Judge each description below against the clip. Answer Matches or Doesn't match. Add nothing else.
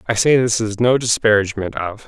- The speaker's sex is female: Doesn't match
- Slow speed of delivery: Doesn't match